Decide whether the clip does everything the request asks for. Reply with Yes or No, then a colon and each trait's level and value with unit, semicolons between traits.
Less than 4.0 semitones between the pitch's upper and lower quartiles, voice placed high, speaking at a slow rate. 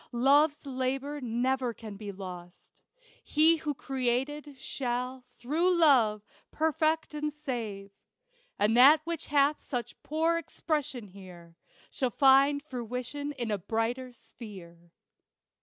No: average, 4.6 semitones; very high, 260 Hz; slow, 115 wpm